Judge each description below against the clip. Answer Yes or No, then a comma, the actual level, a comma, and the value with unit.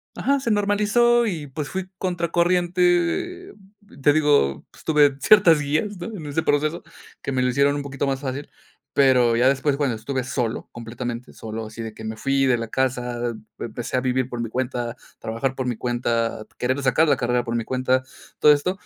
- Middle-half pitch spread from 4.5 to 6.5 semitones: Yes, average, 4.9 semitones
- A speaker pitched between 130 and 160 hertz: Yes, low, 135 Hz